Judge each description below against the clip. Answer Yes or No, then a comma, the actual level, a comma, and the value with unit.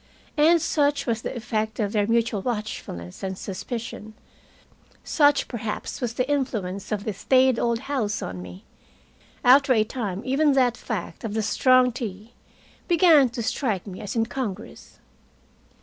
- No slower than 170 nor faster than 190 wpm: No, average, 150 wpm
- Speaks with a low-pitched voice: No, high, 230 Hz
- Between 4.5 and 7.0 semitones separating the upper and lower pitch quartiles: No, average, 3.9 semitones